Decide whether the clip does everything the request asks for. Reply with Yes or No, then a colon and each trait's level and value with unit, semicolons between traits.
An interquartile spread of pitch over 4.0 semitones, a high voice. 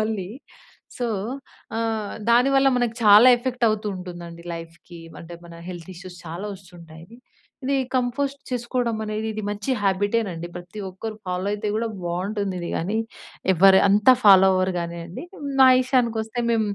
Yes: average, 4.5 semitones; high, 205 Hz